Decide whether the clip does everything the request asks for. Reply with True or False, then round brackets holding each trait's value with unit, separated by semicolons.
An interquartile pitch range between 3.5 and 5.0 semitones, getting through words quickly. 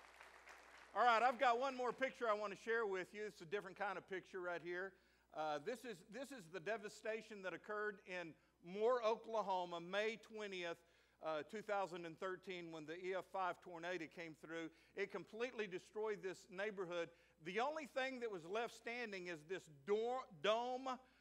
False (4.1 semitones; 165 wpm)